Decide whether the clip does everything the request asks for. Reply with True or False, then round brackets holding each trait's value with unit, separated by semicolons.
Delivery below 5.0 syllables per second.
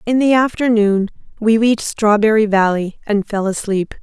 True (4.8 syllables/s)